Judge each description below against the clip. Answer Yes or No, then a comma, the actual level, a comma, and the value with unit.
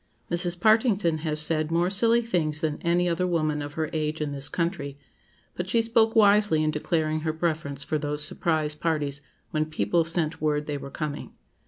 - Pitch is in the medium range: Yes, medium, 160 Hz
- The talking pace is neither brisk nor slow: Yes, average, 185 wpm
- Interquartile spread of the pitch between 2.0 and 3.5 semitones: Yes, narrow, 2.6 semitones